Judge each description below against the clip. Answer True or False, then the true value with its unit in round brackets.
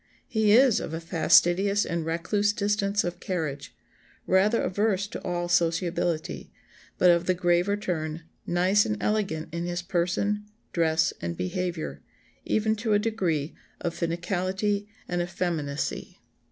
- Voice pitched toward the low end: False (180 Hz)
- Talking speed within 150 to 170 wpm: False (135 wpm)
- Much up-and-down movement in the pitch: False (3.4 semitones)